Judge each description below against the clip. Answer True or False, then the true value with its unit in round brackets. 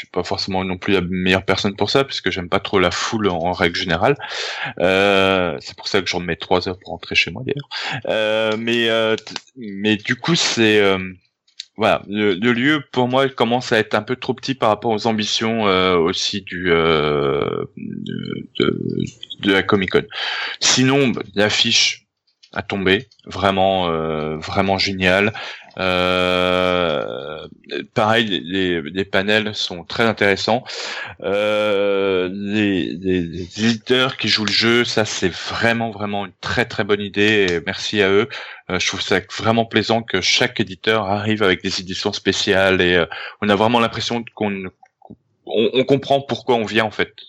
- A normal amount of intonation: True (3.2 semitones)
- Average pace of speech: True (175 wpm)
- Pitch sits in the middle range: False (105 Hz)